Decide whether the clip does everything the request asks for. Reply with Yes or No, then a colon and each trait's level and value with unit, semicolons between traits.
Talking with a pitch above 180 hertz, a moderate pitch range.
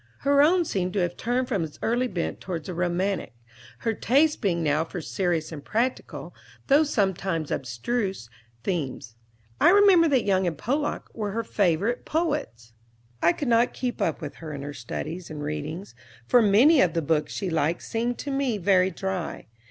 No: high, 190 Hz; wide, 7.0 semitones